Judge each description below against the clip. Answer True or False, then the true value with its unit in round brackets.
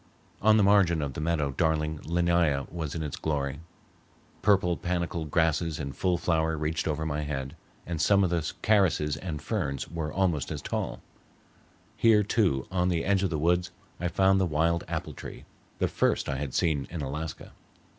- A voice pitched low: True (80 Hz)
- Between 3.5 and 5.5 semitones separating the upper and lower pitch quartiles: False (3.0 semitones)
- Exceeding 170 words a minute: True (180 wpm)